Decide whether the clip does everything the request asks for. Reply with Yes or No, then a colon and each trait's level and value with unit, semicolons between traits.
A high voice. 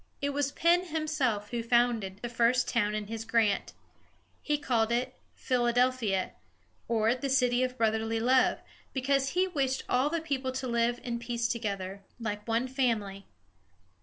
Yes: high, 240 Hz